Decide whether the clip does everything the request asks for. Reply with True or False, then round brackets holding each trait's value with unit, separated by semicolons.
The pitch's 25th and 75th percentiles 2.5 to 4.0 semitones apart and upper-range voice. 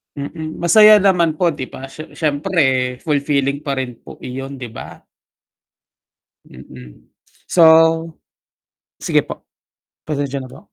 False (3.4 semitones; 140 Hz)